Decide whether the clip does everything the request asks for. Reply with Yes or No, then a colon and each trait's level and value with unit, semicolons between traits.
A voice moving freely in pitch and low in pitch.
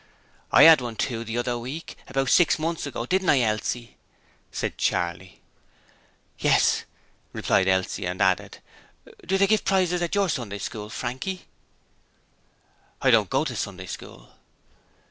Yes: wide, 7.9 semitones; low, 120 Hz